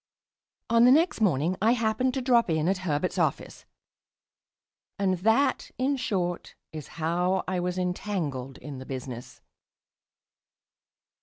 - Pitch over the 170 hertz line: Yes, medium, 185 Hz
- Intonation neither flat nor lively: No, wide, 6.5 semitones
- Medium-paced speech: No, slow, 130 wpm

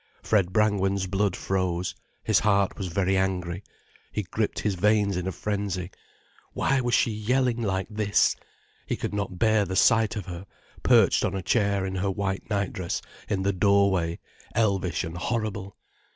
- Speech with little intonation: Yes, narrow, 2.1 semitones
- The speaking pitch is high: No, low, 100 Hz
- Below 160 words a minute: No, average, 165 wpm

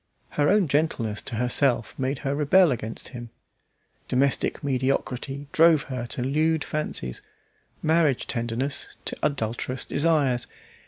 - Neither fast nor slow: No, slow, 120 wpm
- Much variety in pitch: No, average, 3.6 semitones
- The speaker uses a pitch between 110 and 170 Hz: Yes, low, 135 Hz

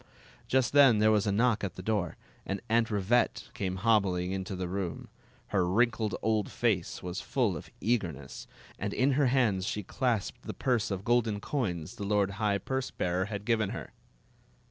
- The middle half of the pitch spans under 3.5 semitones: No, average, 3.8 semitones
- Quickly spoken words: No, average, 180 wpm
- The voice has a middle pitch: No, low, 105 Hz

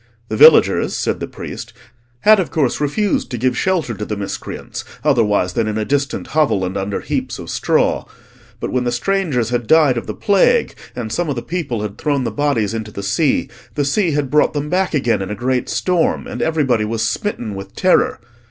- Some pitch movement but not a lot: No, wide, 6.2 semitones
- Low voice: Yes, low, 130 Hz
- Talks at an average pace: No, fast, 210 wpm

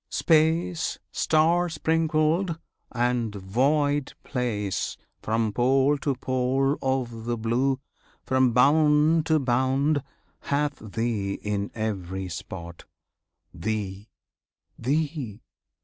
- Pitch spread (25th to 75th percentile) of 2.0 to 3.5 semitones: No, average, 5.2 semitones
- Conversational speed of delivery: No, slow, 90 wpm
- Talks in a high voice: No, low, 130 Hz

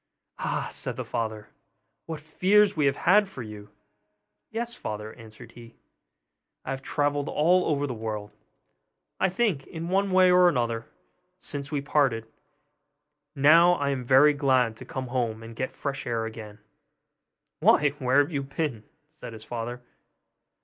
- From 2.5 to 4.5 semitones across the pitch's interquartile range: No, average, 5.2 semitones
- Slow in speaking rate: No, average, 155 wpm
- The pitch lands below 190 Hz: Yes, medium, 140 Hz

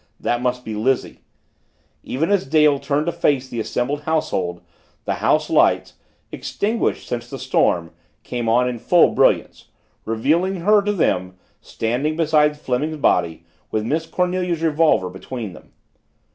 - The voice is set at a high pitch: No, medium, 140 Hz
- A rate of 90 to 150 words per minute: Yes, average, 145 wpm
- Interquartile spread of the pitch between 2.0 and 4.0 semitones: No, wide, 5.6 semitones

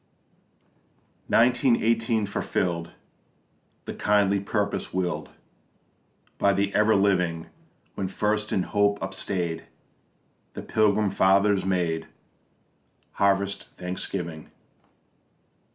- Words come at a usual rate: No, slow, 85 wpm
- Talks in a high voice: No, low, 100 Hz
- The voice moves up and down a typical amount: No, narrow, 2.3 semitones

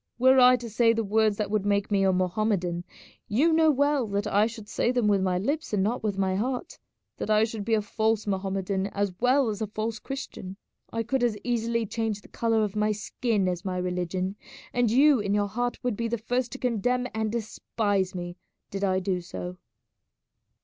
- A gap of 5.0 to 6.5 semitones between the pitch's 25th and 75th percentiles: No, average, 3.3 semitones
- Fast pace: Yes, fast, 210 wpm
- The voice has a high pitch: Yes, high, 215 Hz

